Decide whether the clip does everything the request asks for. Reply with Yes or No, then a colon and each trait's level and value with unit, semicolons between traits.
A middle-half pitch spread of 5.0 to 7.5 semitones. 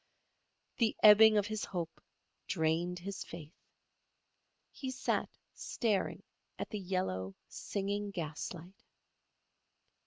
No: average, 3.7 semitones